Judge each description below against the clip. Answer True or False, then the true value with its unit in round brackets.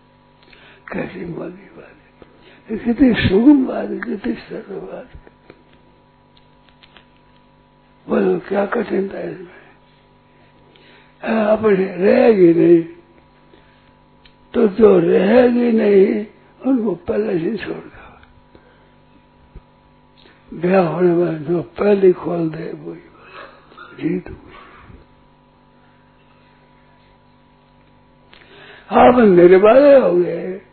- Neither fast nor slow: False (70 wpm)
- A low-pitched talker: False (195 Hz)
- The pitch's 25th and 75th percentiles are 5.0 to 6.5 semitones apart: False (4.1 semitones)